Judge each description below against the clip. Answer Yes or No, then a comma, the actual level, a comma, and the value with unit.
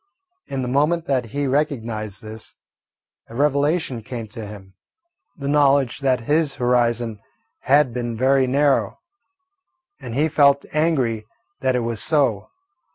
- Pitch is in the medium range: No, low, 130 Hz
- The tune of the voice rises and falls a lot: No, average, 3.7 semitones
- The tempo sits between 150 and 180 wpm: No, slow, 135 wpm